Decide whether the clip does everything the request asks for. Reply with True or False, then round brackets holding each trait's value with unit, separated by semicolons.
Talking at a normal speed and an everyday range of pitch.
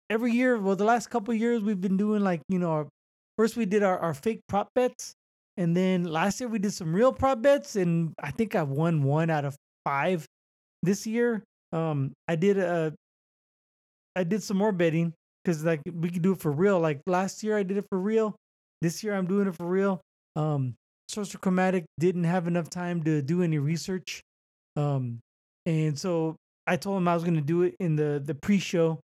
False (215 wpm; 4.1 semitones)